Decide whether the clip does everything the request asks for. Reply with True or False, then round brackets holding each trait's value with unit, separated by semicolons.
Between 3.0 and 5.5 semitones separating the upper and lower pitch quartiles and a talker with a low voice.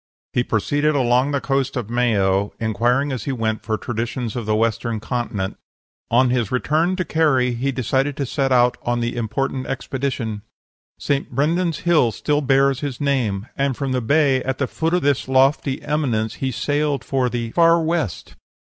True (3.3 semitones; 130 Hz)